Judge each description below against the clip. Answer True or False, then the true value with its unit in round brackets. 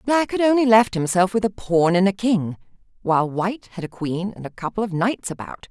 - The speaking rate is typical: False (230 wpm)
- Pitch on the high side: True (200 Hz)